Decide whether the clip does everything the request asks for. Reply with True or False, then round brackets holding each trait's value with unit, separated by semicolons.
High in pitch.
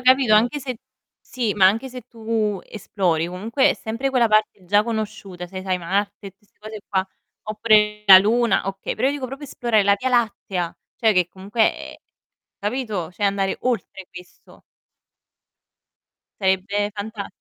True (210 Hz)